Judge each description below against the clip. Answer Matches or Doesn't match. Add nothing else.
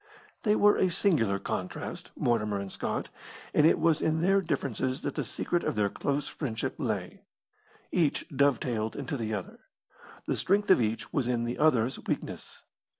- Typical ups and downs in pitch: Doesn't match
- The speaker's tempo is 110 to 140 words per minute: Doesn't match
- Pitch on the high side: Doesn't match